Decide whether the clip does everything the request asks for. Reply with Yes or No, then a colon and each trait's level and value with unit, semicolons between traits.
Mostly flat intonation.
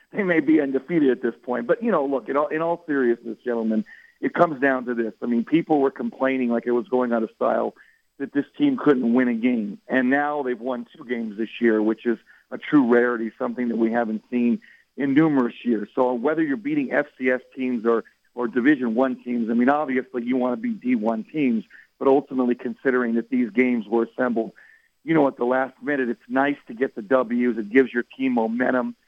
No: average, 3.6 semitones